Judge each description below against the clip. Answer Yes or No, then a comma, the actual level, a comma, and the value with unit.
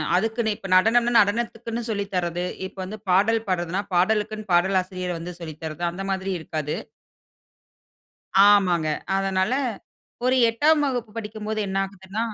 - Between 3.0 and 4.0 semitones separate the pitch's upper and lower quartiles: Yes, average, 3.4 semitones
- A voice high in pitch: Yes, high, 195 Hz